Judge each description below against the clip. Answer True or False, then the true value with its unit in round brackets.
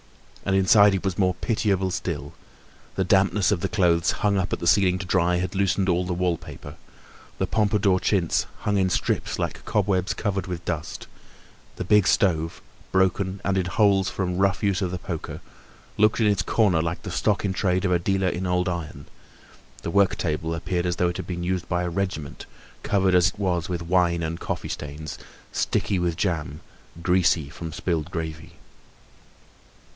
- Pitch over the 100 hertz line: False (90 Hz)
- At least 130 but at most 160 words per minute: False (185 wpm)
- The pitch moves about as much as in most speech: False (2.1 semitones)